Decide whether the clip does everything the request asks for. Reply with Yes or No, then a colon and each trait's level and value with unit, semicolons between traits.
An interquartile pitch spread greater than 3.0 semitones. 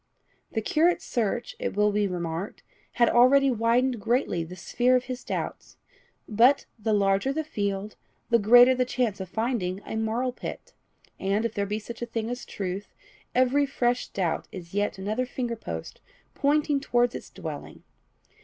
Yes: average, 3.8 semitones